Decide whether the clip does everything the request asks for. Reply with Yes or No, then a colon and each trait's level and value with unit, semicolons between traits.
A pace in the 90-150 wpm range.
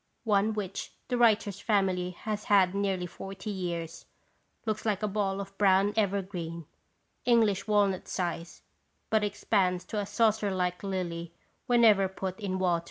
Yes: average, 145 wpm